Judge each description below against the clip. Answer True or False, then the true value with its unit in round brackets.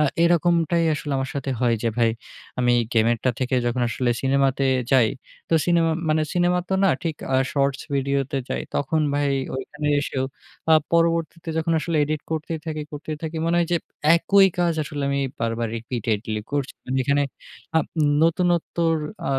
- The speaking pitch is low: False (145 Hz)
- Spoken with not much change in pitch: False (4.1 semitones)